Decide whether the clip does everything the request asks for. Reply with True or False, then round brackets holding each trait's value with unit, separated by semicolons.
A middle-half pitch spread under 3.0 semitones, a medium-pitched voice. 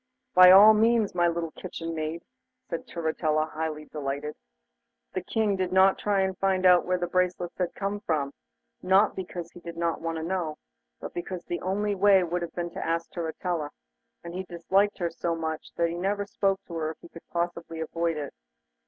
True (2.4 semitones; 175 Hz)